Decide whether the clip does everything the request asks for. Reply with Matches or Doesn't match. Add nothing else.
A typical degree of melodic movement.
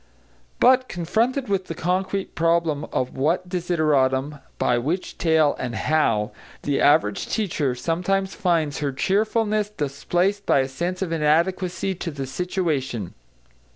Matches